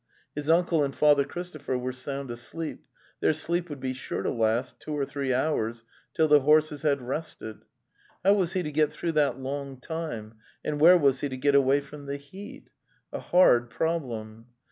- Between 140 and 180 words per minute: No, average, 190 wpm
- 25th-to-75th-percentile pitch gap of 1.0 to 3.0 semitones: No, average, 3.5 semitones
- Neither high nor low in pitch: Yes, medium, 145 Hz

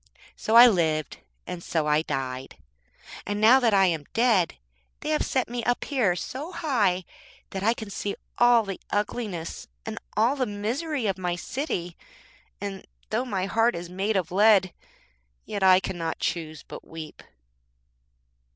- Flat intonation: No, average, 5.2 semitones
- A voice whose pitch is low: No, high, 200 Hz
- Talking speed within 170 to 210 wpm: No, average, 160 wpm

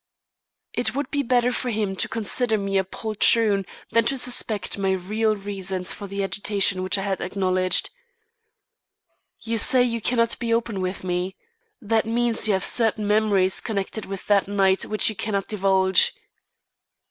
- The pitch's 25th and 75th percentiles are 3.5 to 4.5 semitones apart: No, average, 3.0 semitones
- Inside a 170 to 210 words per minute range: No, average, 160 wpm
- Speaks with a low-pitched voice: No, high, 205 Hz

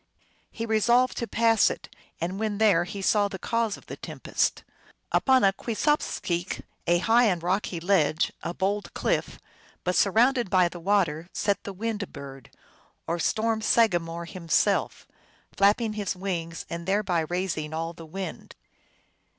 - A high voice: Yes, high, 195 Hz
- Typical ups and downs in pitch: Yes, average, 4.1 semitones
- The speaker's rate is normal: Yes, average, 150 wpm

